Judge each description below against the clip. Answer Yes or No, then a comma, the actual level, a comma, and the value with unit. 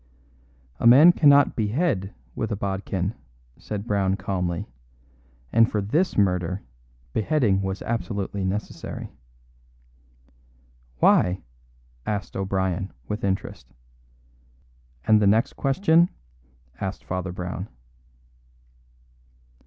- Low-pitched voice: Yes, low, 100 Hz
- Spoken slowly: Yes, slow, 90 wpm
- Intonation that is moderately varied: Yes, average, 3.3 semitones